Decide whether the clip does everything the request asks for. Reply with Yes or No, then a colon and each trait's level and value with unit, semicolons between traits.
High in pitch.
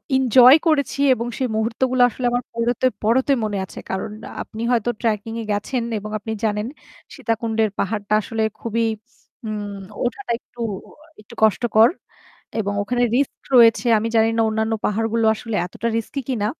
Yes: high, 225 Hz